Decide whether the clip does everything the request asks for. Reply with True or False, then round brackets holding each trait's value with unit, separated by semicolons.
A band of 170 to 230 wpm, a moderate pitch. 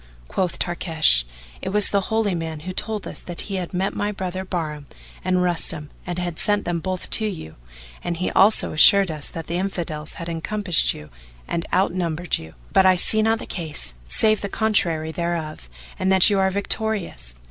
True (190 wpm; 180 Hz)